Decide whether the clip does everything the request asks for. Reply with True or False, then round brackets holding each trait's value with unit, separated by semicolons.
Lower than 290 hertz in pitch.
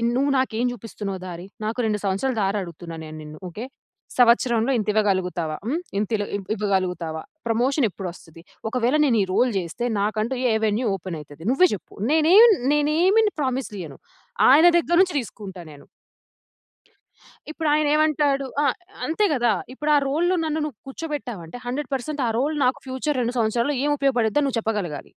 True (240 Hz)